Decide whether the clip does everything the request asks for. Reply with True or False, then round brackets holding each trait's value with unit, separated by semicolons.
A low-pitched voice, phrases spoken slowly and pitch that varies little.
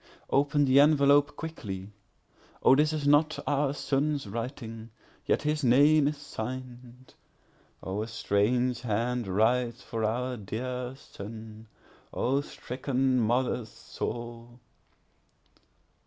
False (125 Hz; 95 wpm; 3.8 semitones)